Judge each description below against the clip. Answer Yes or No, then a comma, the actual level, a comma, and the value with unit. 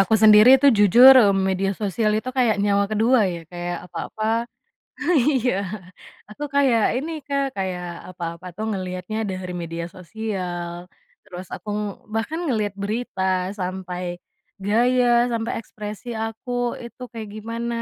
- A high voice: Yes, high, 210 Hz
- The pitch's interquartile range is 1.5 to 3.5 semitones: No, average, 4.2 semitones